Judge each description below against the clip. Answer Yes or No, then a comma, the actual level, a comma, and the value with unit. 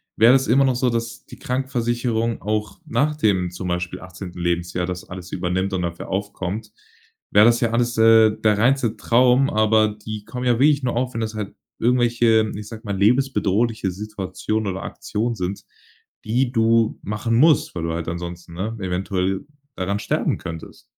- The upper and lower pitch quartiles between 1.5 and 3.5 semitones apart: No, average, 4.1 semitones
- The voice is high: No, low, 110 Hz